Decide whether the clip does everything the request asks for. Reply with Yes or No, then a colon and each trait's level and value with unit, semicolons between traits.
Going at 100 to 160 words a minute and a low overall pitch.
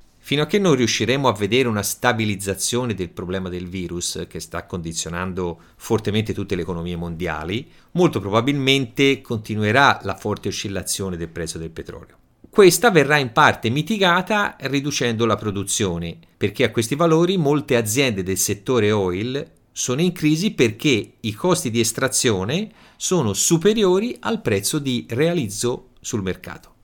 Yes: average, 145 wpm; low, 120 Hz